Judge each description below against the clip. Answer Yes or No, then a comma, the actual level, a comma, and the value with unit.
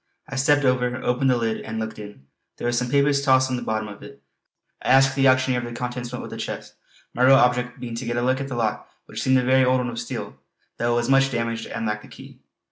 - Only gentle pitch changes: Yes, narrow, 1.9 semitones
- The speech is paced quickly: Yes, fast, 275 wpm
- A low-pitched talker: Yes, low, 125 Hz